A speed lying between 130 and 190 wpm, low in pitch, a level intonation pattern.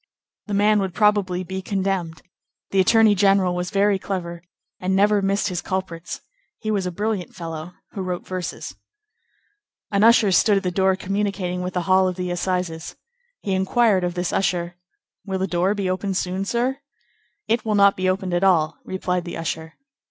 No: average, 180 wpm; high, 190 Hz; narrow, 1.9 semitones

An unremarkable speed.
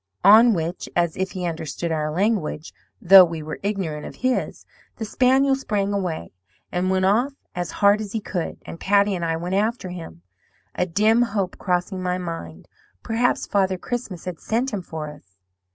Yes: average, 180 wpm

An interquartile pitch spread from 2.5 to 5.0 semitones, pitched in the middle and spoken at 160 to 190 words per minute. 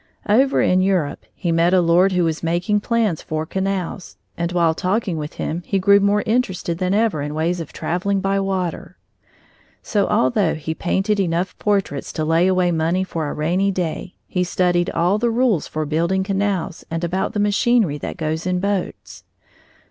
Yes: average, 3.0 semitones; medium, 180 Hz; average, 180 wpm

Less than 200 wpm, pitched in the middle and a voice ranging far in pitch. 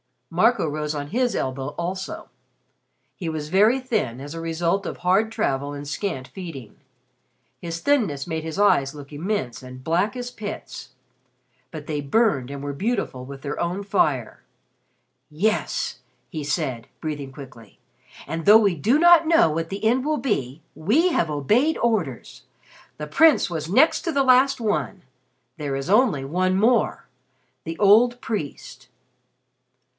Yes: average, 150 wpm; medium, 170 Hz; wide, 7.3 semitones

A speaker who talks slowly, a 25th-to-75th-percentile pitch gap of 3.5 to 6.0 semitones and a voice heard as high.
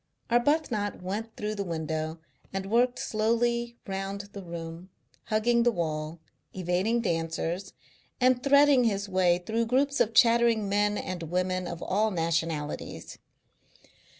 Yes: slow, 125 wpm; average, 5.1 semitones; high, 200 Hz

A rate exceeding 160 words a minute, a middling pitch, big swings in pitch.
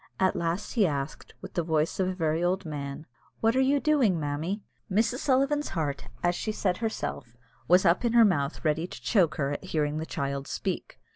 Yes: fast, 205 wpm; medium, 175 Hz; wide, 6.0 semitones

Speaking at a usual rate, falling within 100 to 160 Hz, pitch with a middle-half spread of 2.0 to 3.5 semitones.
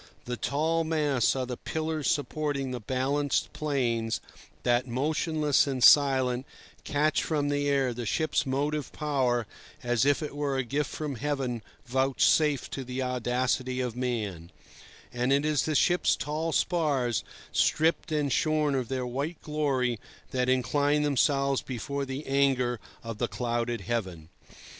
Yes: average, 145 wpm; low, 135 Hz; average, 3.1 semitones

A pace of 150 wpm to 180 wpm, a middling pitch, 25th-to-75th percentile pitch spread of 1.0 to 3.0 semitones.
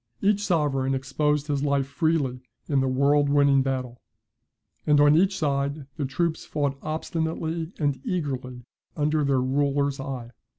No: average, 140 wpm; medium, 145 Hz; narrow, 2.5 semitones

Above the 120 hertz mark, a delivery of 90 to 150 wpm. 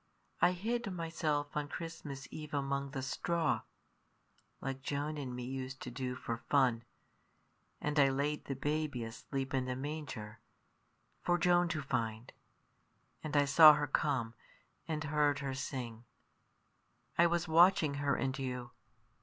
Yes: medium, 140 Hz; average, 145 wpm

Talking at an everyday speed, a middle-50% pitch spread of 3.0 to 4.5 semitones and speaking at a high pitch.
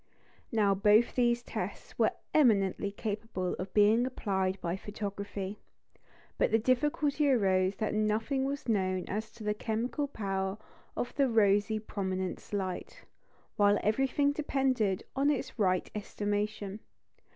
No: slow, 130 wpm; average, 3.6 semitones; high, 210 Hz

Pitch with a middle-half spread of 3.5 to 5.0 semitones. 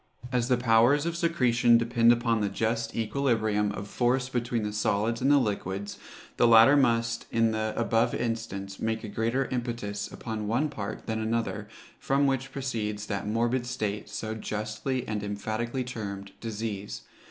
No: narrow, 2.5 semitones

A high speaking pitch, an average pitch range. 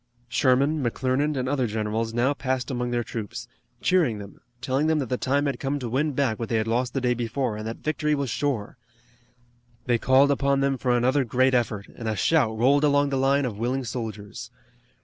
No: low, 130 Hz; average, 3.2 semitones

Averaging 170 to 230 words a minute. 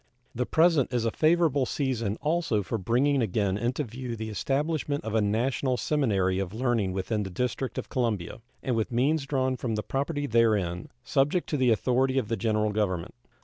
Yes: average, 185 wpm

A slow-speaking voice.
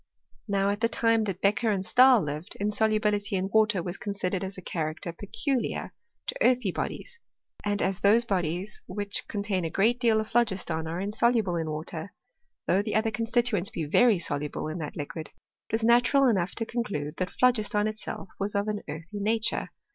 No: average, 195 wpm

